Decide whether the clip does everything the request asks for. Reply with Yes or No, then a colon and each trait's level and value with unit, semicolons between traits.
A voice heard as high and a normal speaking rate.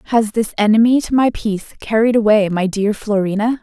Yes: high, 215 Hz; average, 180 wpm